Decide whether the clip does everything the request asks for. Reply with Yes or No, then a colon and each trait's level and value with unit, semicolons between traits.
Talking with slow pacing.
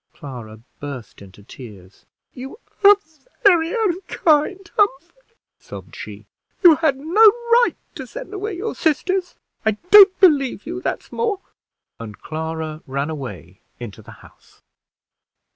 Yes: slow, 125 wpm